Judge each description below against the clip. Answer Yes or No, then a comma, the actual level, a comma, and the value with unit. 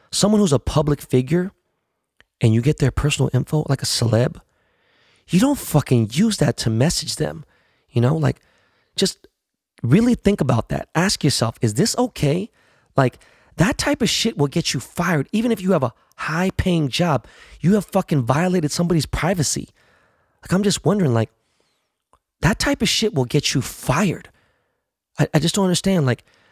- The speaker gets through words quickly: No, average, 175 wpm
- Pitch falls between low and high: Yes, medium, 155 Hz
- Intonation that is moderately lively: No, wide, 6.6 semitones